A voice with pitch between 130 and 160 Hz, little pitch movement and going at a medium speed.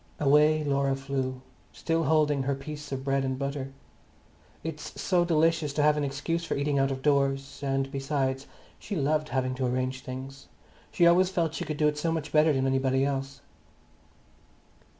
Yes: medium, 140 Hz; narrow, 2.2 semitones; average, 175 wpm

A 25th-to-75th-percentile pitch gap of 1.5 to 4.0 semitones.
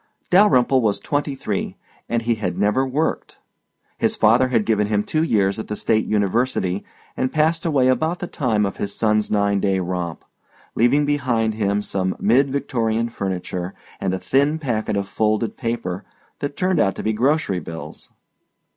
No: average, 4.9 semitones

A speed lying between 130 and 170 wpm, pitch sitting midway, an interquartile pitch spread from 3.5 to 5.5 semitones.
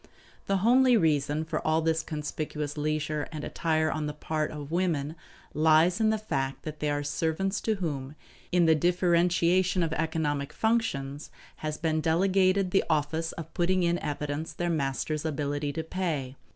No: average, 165 wpm; medium, 160 Hz; average, 2.9 semitones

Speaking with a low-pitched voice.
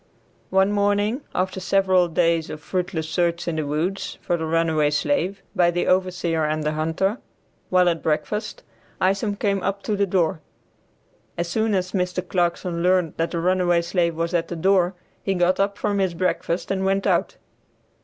No: medium, 180 Hz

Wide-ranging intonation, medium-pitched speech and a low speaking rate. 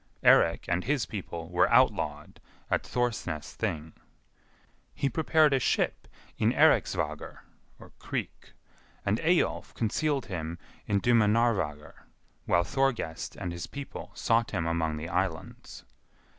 No: wide, 6.5 semitones; low, 100 Hz; slow, 115 wpm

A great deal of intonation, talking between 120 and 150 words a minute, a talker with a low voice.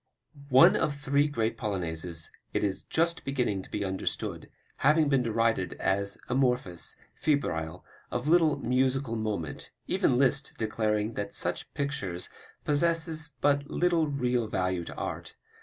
Yes: wide, 6.1 semitones; slow, 135 wpm; low, 125 Hz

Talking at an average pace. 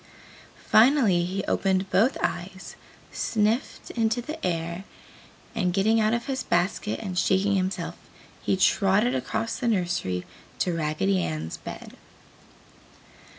No: slow, 120 wpm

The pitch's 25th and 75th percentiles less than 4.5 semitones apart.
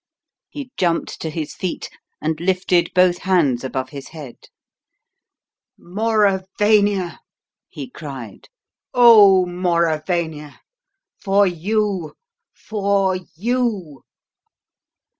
Yes: average, 3.9 semitones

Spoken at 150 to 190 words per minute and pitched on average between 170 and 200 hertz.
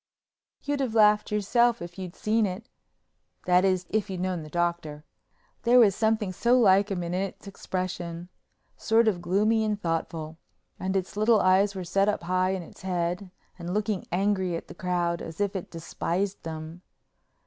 Yes: average, 160 wpm; high, 190 Hz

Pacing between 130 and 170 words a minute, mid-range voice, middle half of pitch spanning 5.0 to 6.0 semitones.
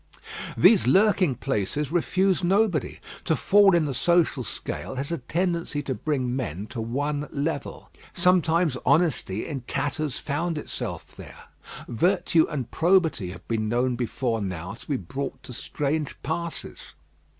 Yes: average, 140 wpm; medium, 145 Hz; wide, 5.4 semitones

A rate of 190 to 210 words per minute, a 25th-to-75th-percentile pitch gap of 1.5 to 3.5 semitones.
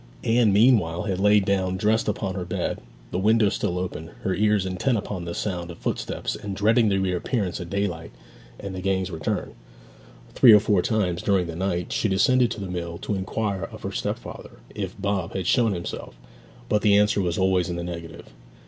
Yes: average, 195 wpm; average, 2.8 semitones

